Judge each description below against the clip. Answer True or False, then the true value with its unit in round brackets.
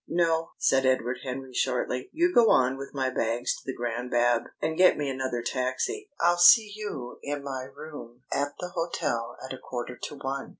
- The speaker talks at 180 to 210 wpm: True (190 wpm)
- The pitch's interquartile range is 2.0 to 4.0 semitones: False (4.5 semitones)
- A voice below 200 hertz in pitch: True (135 Hz)